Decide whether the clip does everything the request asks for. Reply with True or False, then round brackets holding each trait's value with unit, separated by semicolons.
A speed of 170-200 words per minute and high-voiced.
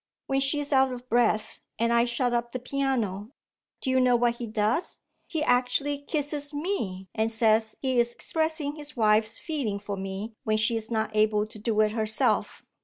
True (190 wpm; 235 Hz)